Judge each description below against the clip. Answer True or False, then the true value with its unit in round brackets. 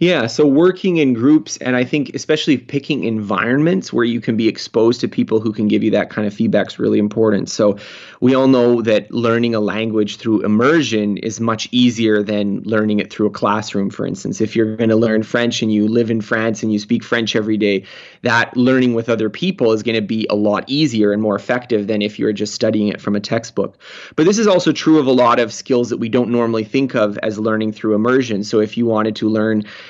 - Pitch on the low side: True (110 Hz)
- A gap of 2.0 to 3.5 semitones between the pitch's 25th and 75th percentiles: True (2.5 semitones)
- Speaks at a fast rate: True (235 wpm)